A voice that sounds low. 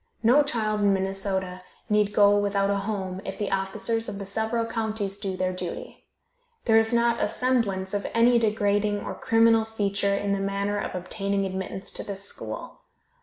No: high, 205 Hz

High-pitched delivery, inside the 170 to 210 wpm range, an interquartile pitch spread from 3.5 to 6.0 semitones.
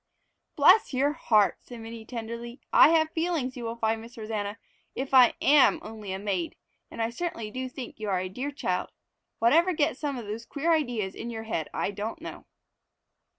Yes: high, 235 Hz; average, 195 wpm; average, 4.6 semitones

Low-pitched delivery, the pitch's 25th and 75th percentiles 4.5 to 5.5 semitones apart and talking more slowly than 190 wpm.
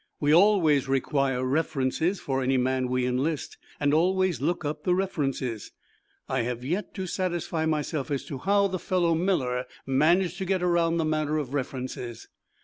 No: medium, 155 Hz; average, 5.0 semitones; average, 165 wpm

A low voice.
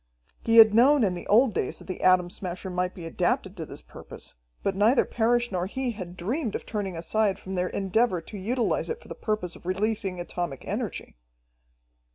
No: high, 195 Hz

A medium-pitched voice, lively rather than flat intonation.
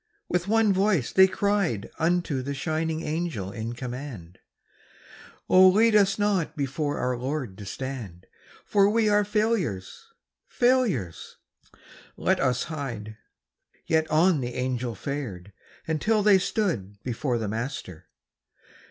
Yes: medium, 150 Hz; wide, 8.2 semitones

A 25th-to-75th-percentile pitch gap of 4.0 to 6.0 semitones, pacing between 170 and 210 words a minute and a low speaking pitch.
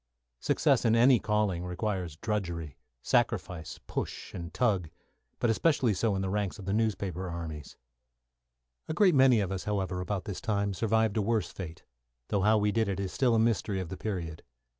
No: average, 3.5 semitones; average, 185 wpm; low, 100 Hz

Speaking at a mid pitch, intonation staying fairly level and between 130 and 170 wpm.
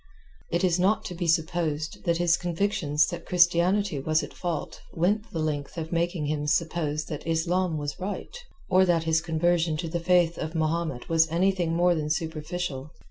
No: medium, 165 Hz; narrow, 2.1 semitones; average, 180 wpm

